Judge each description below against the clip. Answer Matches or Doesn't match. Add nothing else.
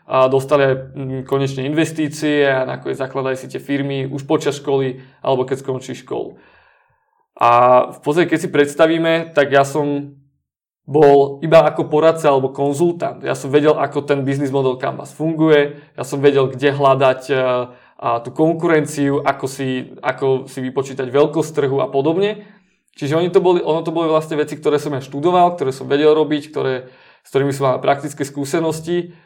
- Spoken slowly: Doesn't match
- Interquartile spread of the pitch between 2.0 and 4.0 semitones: Matches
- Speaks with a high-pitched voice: Doesn't match